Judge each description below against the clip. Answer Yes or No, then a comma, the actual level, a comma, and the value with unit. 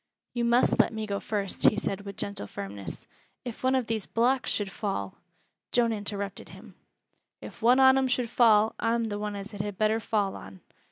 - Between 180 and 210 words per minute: Yes, fast, 205 wpm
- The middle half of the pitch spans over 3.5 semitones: No, average, 2.8 semitones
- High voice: Yes, high, 215 Hz